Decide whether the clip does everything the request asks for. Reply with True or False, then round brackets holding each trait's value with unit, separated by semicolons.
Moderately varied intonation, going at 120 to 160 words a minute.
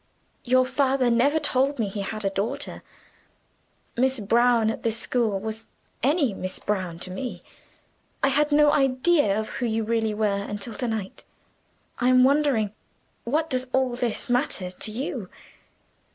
True (3.8 semitones; 150 wpm)